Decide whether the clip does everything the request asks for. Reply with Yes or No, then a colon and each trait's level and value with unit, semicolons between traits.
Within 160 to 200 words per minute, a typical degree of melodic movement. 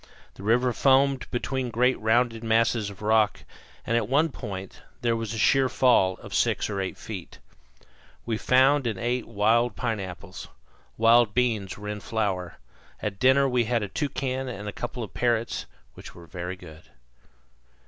Yes: average, 165 wpm; average, 3.4 semitones